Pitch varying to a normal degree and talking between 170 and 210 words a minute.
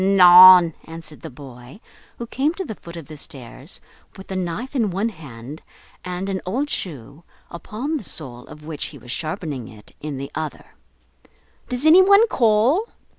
No: wide, 7.2 semitones; average, 175 wpm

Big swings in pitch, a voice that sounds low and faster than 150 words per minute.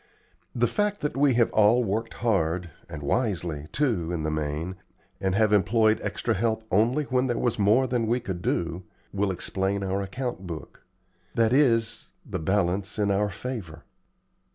No: average, 4.6 semitones; low, 105 Hz; average, 165 wpm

